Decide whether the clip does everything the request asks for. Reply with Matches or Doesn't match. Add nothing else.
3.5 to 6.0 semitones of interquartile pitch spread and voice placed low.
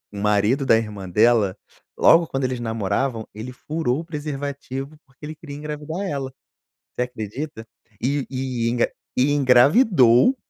Matches